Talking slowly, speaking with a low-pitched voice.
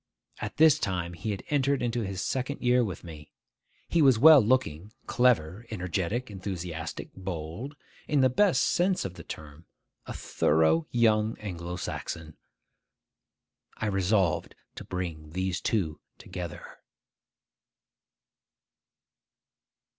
Yes: slow, 115 wpm; very low, 95 Hz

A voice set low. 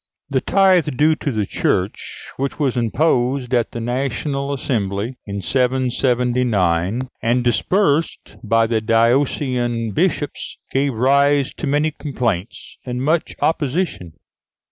Yes: low, 125 Hz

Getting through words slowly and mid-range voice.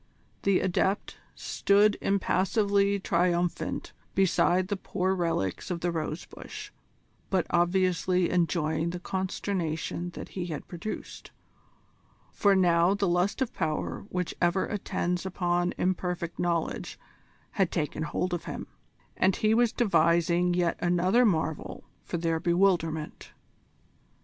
Yes: slow, 120 wpm; medium, 180 Hz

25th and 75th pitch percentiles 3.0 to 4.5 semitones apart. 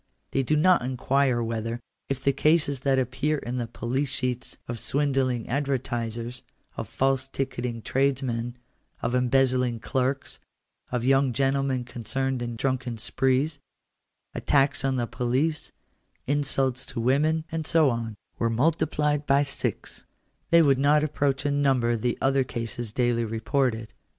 No: narrow, 2.5 semitones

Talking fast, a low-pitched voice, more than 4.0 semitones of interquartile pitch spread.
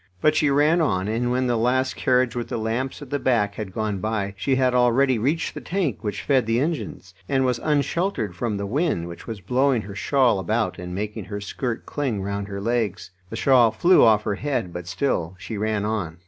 Yes: fast, 215 wpm; low, 115 Hz; average, 4.6 semitones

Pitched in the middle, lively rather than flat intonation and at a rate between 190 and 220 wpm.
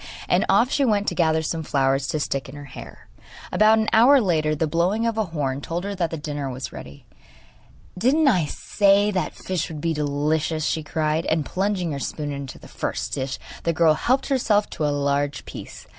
Yes: medium, 160 Hz; wide, 5.7 semitones; average, 200 wpm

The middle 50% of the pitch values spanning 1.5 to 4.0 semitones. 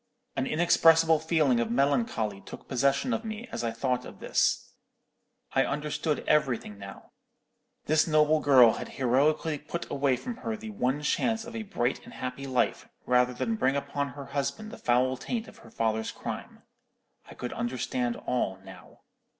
No: average, 4.6 semitones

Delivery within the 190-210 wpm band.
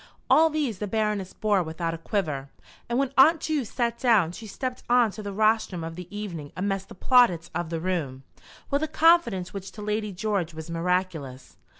Yes: average, 195 wpm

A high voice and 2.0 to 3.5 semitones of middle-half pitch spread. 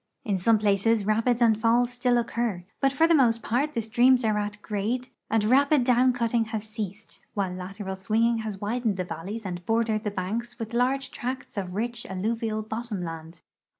Yes: high, 225 Hz; average, 2.9 semitones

